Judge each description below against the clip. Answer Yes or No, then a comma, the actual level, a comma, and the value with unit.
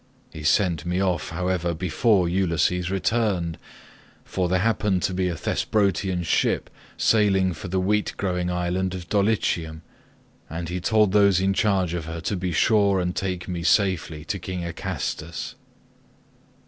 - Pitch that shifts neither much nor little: No, narrow, 2.2 semitones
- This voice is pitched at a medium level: No, very low, 90 Hz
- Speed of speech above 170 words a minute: No, average, 150 wpm